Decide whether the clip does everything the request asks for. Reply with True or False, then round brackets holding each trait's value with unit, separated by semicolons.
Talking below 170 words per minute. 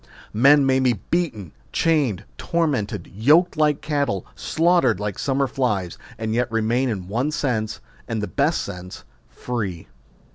True (140 wpm)